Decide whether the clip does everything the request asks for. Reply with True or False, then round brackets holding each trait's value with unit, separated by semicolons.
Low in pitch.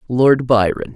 True (120 Hz)